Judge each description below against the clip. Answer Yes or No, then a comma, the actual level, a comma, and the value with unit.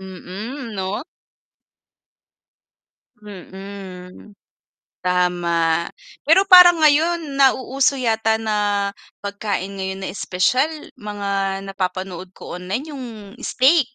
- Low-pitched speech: No, high, 200 Hz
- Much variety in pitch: Yes, wide, 5.8 semitones